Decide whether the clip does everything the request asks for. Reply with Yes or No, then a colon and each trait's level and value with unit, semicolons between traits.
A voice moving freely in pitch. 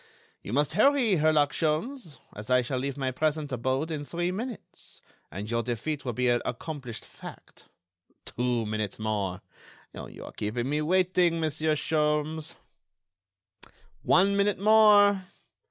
Yes: wide, 6.2 semitones